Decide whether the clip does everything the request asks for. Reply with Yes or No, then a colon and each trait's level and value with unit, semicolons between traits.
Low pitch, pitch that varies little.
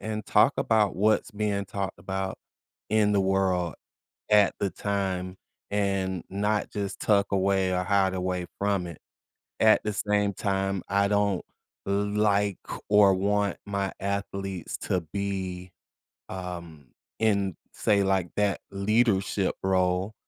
Yes: low, 100 Hz; narrow, 1.5 semitones